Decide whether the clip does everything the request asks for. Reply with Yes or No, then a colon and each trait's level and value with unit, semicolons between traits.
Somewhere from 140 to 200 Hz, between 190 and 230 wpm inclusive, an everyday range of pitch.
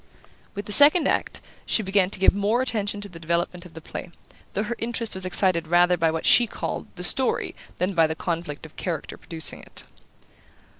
Yes: medium, 185 Hz; average, 200 wpm; average, 3.6 semitones